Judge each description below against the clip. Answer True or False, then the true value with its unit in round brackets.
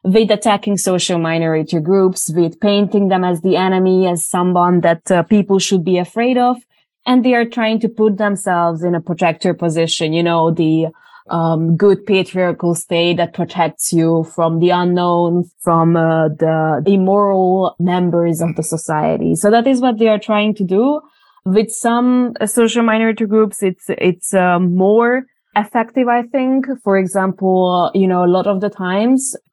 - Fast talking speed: False (165 wpm)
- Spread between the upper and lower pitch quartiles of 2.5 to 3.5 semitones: False (3.9 semitones)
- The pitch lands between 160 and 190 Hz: True (185 Hz)